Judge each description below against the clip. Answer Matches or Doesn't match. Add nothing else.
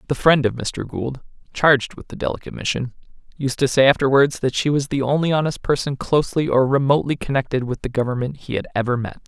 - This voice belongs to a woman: Doesn't match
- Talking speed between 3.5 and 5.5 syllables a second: Doesn't match